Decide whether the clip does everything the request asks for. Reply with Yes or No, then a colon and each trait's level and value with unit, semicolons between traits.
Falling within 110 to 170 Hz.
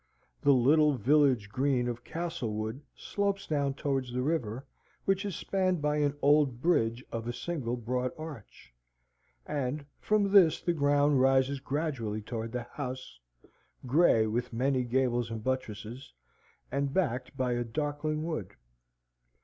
Yes: low, 135 Hz